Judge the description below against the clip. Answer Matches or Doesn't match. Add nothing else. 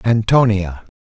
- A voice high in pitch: Doesn't match